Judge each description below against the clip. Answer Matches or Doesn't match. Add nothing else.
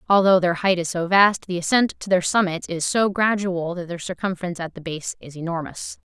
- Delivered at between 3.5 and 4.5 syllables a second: Doesn't match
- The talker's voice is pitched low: Doesn't match